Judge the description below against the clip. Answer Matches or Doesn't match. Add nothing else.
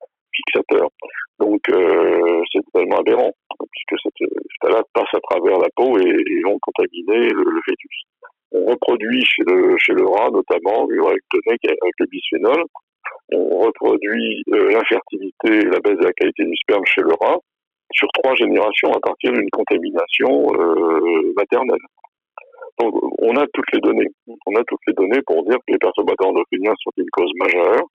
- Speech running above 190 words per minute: Doesn't match